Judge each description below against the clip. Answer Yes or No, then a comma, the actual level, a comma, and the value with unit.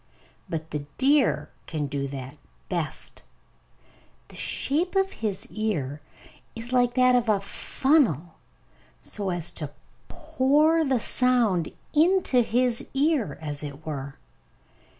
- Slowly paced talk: Yes, slow, 120 wpm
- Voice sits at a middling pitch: No, high, 230 Hz